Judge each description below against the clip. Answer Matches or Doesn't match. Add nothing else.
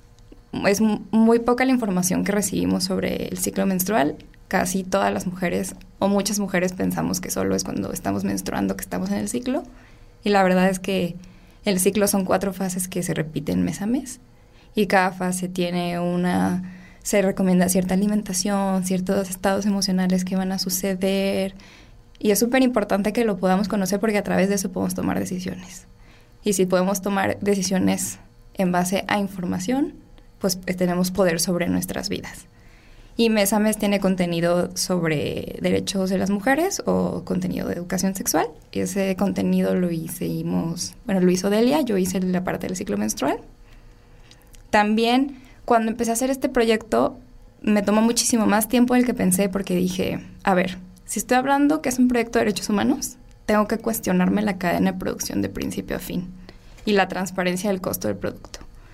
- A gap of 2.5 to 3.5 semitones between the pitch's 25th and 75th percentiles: Matches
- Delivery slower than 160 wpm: Doesn't match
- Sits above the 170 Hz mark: Matches